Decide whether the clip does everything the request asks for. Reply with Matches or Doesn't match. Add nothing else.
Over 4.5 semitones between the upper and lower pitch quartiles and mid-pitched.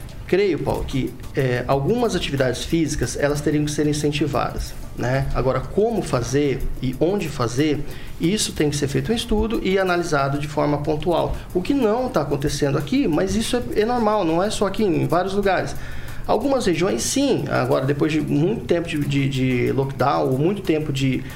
Matches